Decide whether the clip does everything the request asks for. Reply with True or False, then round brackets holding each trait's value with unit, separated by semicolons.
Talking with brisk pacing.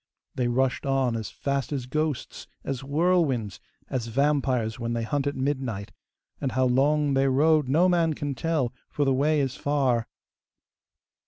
False (160 wpm)